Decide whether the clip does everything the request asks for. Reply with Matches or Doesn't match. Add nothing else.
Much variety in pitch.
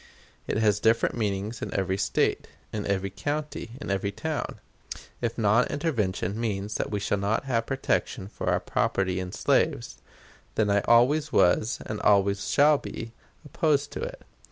Doesn't match